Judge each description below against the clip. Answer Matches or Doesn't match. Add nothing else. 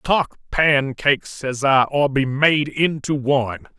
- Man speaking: Matches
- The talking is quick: Doesn't match